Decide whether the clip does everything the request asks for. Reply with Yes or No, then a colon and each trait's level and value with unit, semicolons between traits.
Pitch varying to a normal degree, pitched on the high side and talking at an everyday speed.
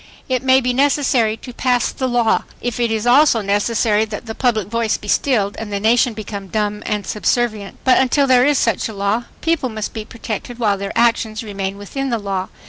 No: average, 3.0 semitones; high, 225 Hz; fast, 210 wpm